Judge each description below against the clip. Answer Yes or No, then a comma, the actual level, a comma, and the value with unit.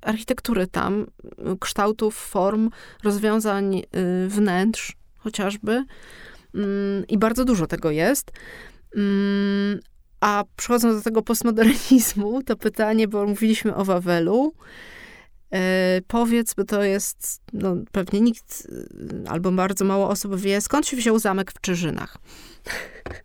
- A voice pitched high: Yes, high, 205 Hz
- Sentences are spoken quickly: No, average, 115 wpm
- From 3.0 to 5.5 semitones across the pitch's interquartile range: No, narrow, 2.5 semitones